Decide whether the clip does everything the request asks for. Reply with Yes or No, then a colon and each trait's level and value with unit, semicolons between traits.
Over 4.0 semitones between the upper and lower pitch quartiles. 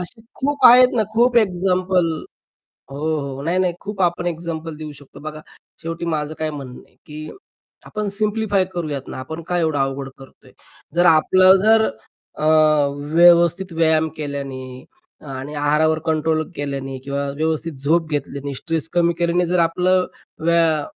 No: average, 3.4 semitones